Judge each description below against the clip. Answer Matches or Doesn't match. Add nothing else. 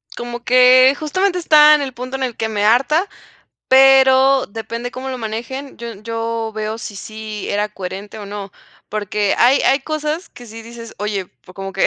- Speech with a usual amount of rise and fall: Matches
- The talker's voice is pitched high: Matches